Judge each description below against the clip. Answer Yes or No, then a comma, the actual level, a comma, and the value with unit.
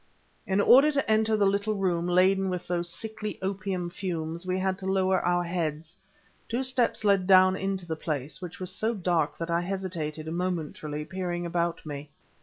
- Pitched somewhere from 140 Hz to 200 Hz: Yes, medium, 185 Hz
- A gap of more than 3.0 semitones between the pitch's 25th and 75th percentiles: No, narrow, 2.5 semitones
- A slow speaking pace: No, average, 180 wpm